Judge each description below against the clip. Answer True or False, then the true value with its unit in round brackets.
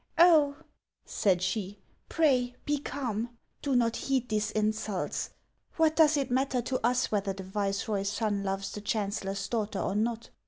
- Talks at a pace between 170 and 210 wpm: True (180 wpm)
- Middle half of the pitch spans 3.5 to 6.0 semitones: True (4.5 semitones)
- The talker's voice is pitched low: False (220 Hz)